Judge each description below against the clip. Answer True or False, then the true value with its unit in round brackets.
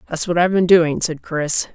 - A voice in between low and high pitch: True (165 Hz)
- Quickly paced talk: True (240 wpm)